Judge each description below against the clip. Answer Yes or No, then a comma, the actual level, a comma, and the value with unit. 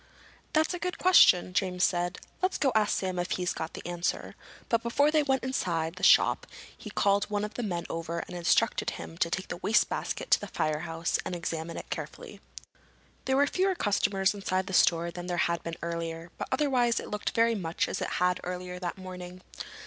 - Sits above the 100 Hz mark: Yes, medium, 185 Hz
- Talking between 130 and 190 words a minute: No, average, 200 wpm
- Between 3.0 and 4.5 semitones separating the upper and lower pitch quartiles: No, average, 5.1 semitones